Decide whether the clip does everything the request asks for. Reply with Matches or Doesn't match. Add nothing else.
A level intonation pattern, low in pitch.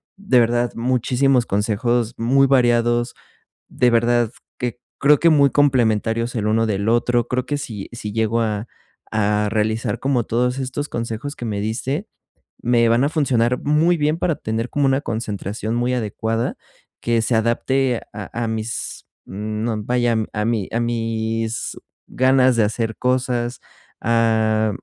Matches